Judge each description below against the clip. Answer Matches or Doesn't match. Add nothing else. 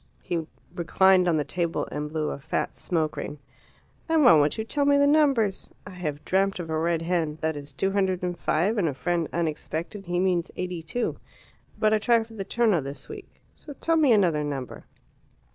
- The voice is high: Doesn't match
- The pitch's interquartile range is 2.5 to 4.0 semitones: Doesn't match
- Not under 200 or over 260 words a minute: Matches